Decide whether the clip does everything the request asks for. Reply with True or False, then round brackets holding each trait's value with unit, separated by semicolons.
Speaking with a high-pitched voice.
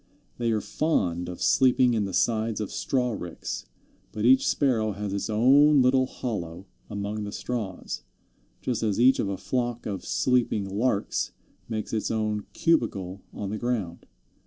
False (110 Hz)